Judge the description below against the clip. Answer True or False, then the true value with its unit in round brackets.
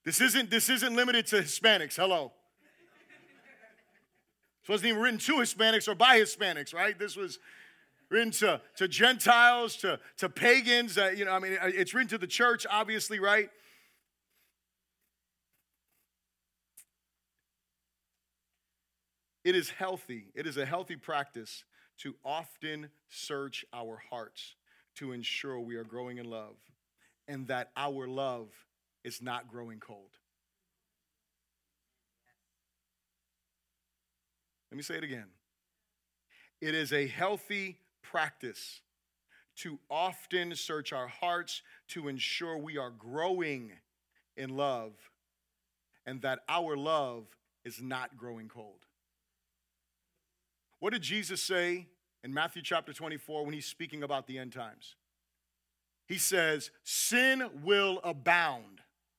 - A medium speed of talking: False (120 wpm)